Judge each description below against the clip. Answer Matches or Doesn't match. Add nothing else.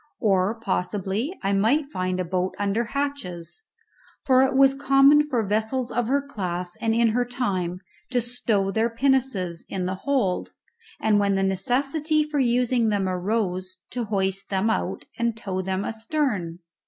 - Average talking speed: Matches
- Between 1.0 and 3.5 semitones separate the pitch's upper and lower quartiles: Doesn't match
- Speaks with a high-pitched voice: Matches